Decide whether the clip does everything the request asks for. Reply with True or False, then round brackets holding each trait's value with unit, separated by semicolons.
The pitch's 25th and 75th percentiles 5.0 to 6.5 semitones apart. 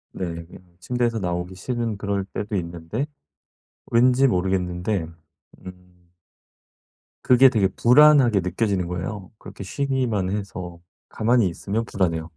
False (4.6 semitones)